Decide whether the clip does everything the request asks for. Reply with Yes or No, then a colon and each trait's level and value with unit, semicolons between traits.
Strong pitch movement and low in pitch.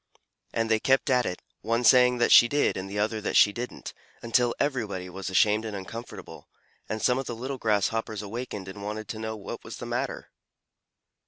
No: average, 2.9 semitones; low, 110 Hz